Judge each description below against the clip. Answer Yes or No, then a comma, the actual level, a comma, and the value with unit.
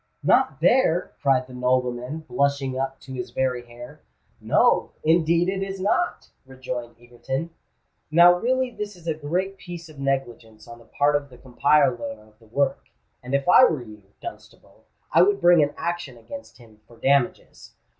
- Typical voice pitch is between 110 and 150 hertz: Yes, medium, 140 Hz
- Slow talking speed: No, average, 165 wpm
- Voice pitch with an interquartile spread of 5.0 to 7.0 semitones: Yes, wide, 5.6 semitones